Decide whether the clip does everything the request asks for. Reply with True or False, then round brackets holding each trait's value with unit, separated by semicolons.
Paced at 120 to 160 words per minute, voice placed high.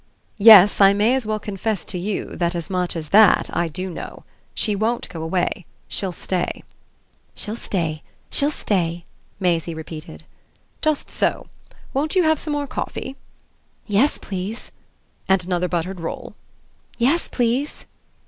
True (145 wpm; 195 Hz)